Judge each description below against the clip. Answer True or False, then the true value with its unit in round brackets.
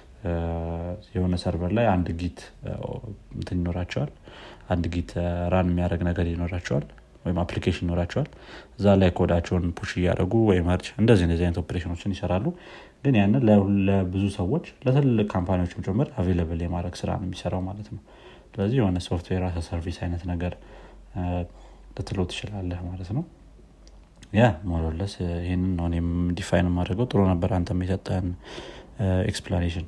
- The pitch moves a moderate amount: False (2.3 semitones)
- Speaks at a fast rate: True (125 wpm)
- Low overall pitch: True (90 Hz)